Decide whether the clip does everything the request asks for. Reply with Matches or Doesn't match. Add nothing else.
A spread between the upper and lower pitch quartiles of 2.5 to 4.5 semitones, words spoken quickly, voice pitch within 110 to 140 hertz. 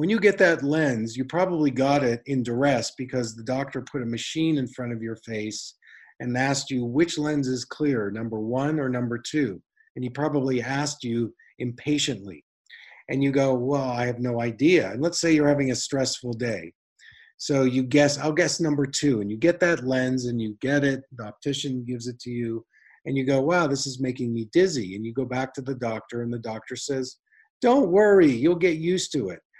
Matches